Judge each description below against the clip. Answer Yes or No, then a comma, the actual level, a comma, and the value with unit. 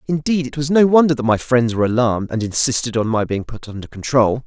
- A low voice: Yes, low, 125 Hz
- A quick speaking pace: Yes, fast, 240 wpm